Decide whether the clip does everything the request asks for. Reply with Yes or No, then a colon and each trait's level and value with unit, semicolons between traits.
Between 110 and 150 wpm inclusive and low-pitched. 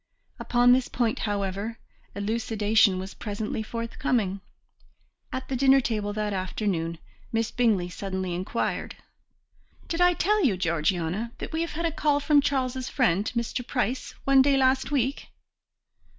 No: slow, 135 wpm; high, 230 Hz